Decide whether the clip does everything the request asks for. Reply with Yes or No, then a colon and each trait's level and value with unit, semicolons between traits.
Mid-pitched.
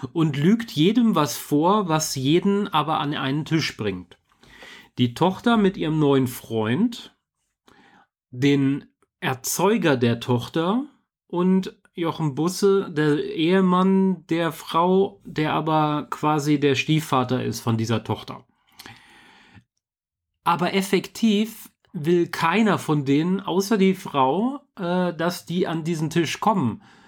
Yes: medium, 165 Hz